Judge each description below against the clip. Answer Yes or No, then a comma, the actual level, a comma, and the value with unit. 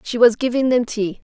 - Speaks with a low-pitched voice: No, high, 235 Hz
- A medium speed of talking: No, fast, 230 wpm